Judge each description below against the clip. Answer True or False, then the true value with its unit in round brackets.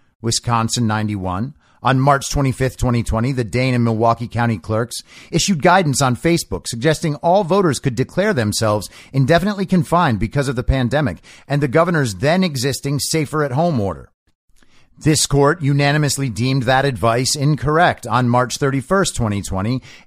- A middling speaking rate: True (155 wpm)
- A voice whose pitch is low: True (130 Hz)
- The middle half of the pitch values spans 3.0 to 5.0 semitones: True (4.3 semitones)